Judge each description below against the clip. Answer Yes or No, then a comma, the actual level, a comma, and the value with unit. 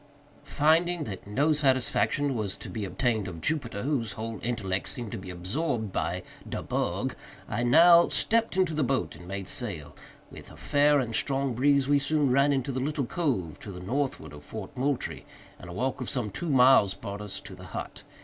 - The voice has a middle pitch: No, low, 125 Hz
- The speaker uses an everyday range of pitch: No, wide, 6.0 semitones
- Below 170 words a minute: No, average, 195 wpm